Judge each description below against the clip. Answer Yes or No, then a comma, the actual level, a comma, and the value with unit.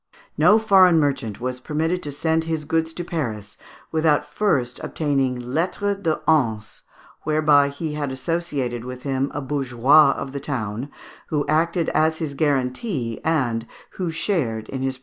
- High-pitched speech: No, medium, 145 Hz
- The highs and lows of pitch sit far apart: No, average, 4.1 semitones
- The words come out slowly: No, average, 155 wpm